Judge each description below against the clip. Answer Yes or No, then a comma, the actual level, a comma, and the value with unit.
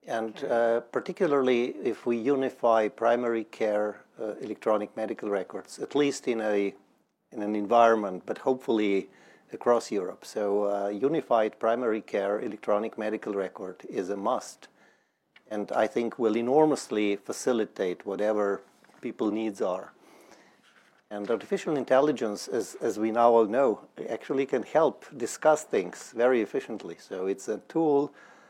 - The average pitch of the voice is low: Yes, low, 115 Hz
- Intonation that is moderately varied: Yes, average, 3.9 semitones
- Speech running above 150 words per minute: No, slow, 135 wpm